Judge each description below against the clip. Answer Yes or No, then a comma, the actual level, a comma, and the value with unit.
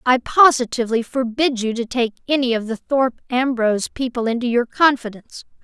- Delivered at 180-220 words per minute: No, average, 160 wpm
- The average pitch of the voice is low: No, high, 245 Hz